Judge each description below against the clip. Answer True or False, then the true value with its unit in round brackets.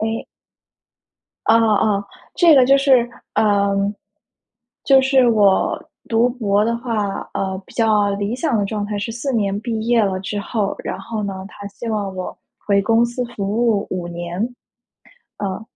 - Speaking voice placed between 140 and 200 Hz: False (210 Hz)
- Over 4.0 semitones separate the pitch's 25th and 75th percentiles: False (2.8 semitones)